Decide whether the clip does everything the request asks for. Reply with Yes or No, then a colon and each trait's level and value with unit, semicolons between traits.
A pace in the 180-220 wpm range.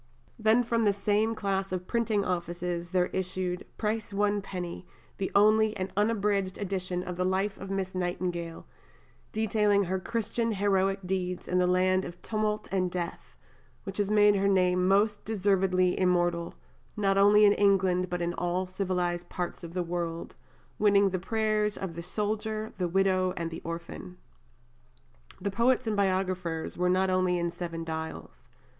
No: average, 160 wpm